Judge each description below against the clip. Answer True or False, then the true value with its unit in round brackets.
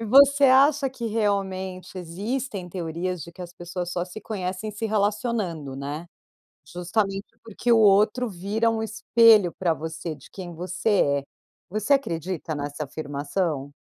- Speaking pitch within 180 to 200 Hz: True (190 Hz)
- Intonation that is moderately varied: True (4.6 semitones)